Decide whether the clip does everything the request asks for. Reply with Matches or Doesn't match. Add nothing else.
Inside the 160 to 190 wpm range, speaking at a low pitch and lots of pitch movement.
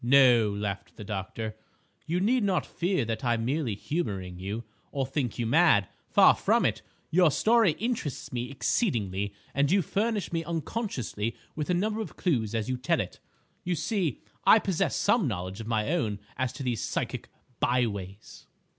Matches